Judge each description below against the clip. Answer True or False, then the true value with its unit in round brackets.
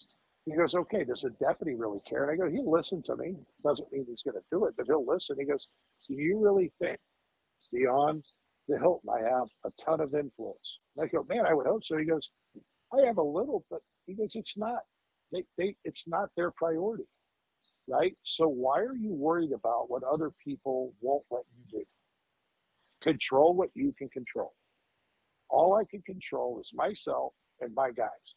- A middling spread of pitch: False (6.3 semitones)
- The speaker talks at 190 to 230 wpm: True (195 wpm)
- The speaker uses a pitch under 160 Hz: False (165 Hz)